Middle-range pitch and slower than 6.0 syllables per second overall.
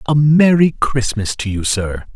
No: low, 130 Hz; 4.2 syllables/s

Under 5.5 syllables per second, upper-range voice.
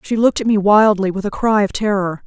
No: 6.0 syllables/s; high, 205 Hz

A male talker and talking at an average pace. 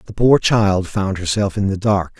No: male; fast, 220 wpm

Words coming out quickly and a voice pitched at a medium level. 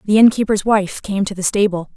No: fast, 245 wpm; high, 200 Hz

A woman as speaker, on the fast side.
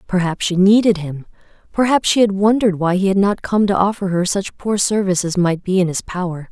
Yes: female; fast, 220 wpm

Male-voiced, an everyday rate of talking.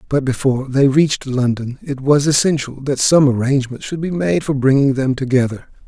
Yes: male; average, 185 wpm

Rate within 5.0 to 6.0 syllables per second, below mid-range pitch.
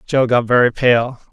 No: 4.6 syllables/s; low, 120 Hz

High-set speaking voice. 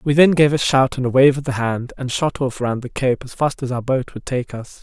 No: low, 130 Hz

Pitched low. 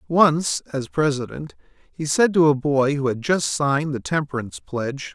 No: medium, 145 Hz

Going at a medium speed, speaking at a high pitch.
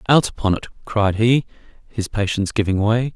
No: average, 170 wpm; low, 110 Hz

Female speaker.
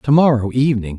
No: male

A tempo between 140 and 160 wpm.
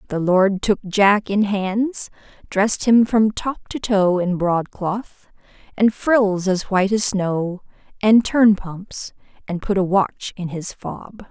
Yes: average, 155 wpm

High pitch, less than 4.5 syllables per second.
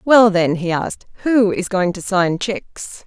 Yes: high, 195 Hz; 4.3 syllables/s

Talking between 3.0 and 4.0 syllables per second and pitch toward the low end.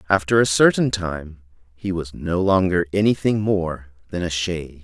No: 4.7 syllables/s; very low, 90 Hz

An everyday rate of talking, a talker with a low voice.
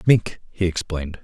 Yes: average, 145 wpm; very low, 90 Hz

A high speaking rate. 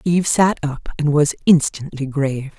No: average, 160 wpm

